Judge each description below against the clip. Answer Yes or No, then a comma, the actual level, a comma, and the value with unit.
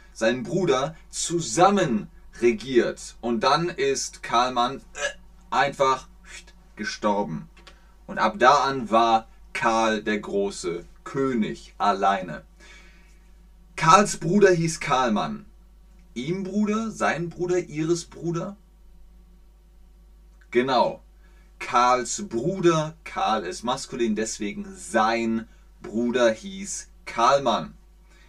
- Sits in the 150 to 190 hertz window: Yes, medium, 185 Hz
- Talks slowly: Yes, slow, 90 wpm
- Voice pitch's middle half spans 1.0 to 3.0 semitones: Yes, average, 2.7 semitones